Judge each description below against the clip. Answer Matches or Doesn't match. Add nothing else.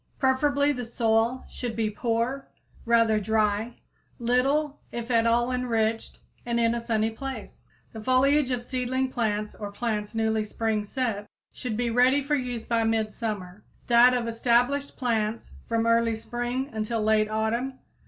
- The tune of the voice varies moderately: Doesn't match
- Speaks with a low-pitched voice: Doesn't match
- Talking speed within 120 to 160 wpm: Matches